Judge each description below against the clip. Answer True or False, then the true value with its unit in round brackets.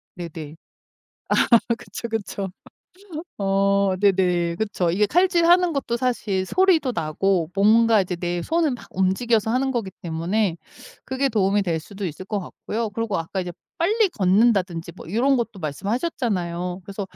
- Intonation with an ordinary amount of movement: True (4.8 semitones)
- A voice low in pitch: False (200 Hz)